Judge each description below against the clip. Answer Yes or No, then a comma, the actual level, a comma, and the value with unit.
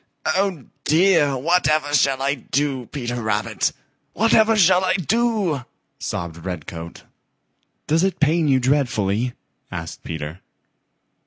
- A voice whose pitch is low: No, medium, 145 Hz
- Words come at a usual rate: No, slow, 110 wpm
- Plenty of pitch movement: Yes, wide, 6.8 semitones